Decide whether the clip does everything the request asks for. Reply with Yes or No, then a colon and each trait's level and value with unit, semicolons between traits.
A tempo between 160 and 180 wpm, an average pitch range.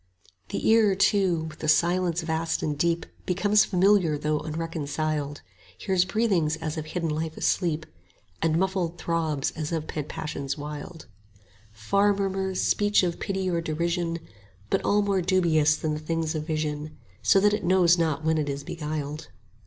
Yes: average, 170 wpm; average, 3.2 semitones